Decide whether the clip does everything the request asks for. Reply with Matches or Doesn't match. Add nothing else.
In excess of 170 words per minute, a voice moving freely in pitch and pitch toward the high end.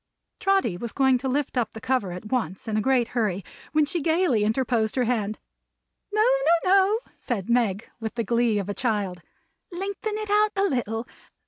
Matches